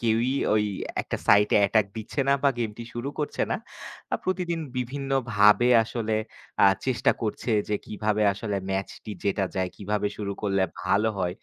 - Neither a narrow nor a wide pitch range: Yes, average, 3.0 semitones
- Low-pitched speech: Yes, low, 110 Hz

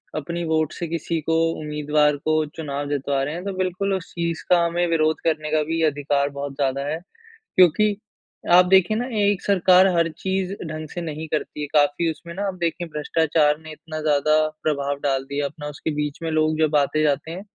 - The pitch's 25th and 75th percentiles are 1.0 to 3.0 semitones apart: Yes, narrow, 2.5 semitones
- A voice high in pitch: No, medium, 155 Hz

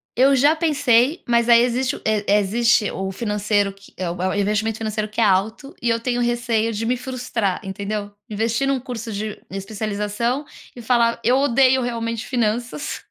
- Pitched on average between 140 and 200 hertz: No, high, 230 Hz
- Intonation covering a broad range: No, average, 2.8 semitones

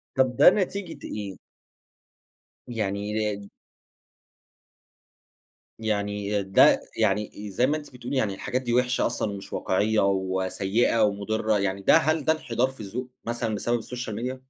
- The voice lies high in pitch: No, low, 110 Hz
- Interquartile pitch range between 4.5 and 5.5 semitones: No, average, 3.8 semitones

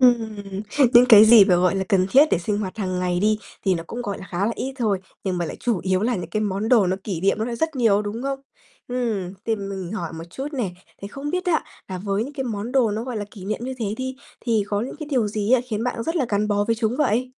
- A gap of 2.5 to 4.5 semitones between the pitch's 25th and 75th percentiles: Yes, average, 3.9 semitones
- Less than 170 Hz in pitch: No, high, 215 Hz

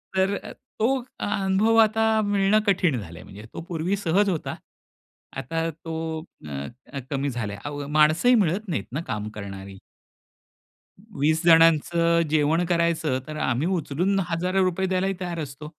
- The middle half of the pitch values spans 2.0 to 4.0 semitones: No, average, 4.9 semitones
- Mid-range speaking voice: Yes, medium, 165 Hz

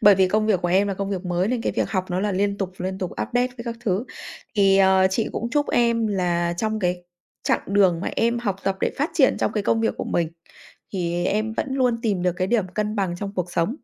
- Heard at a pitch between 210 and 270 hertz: No, high, 200 Hz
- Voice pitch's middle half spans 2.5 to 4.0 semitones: Yes, average, 3.5 semitones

